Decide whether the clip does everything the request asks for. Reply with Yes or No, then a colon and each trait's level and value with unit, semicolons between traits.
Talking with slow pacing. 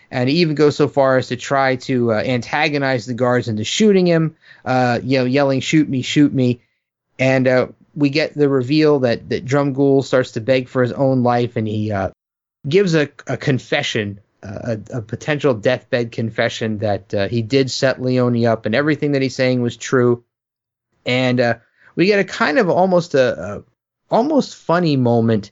No: average, 195 wpm